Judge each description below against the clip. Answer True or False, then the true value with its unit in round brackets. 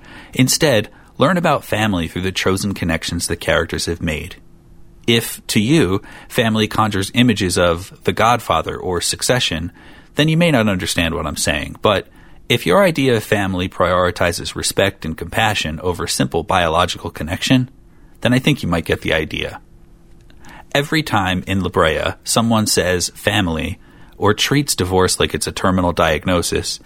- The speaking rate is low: False (150 wpm)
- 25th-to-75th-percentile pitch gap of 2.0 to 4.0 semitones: False (4.6 semitones)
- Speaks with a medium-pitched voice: False (95 Hz)